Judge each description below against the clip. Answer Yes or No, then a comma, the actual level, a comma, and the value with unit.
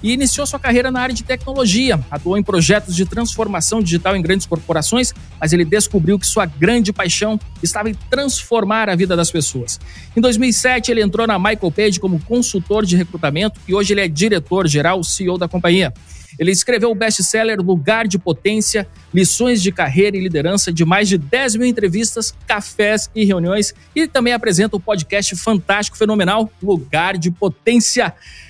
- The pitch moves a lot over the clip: No, average, 3.9 semitones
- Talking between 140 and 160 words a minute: No, average, 175 wpm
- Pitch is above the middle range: Yes, high, 200 Hz